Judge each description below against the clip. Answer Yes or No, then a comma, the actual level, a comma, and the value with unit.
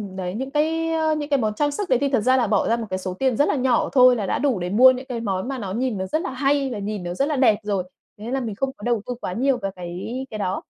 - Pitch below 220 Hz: No, high, 245 Hz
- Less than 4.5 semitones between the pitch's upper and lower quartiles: No, average, 5.0 semitones